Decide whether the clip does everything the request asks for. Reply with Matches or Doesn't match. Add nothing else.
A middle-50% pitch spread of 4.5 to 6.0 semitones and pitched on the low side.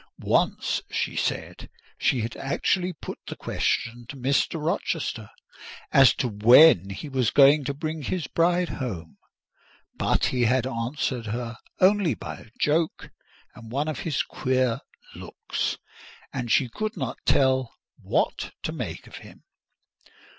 Matches